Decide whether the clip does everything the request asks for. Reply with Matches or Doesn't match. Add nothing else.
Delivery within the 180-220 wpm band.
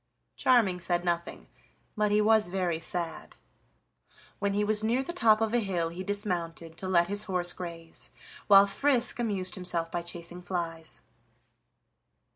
Doesn't match